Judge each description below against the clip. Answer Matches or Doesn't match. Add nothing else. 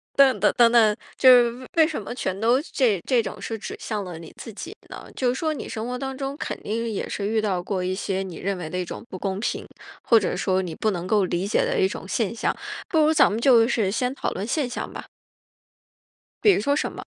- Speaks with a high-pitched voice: Matches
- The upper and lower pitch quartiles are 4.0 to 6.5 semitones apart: Matches